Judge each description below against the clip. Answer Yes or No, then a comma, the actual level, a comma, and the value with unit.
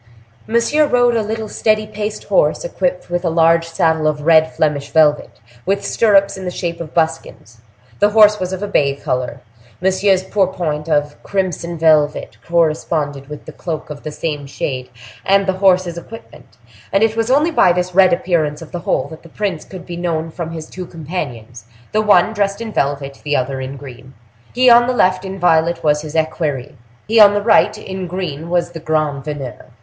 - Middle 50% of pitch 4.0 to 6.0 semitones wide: Yes, average, 4.6 semitones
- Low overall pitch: No, medium, 170 Hz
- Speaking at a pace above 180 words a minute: Yes, average, 195 wpm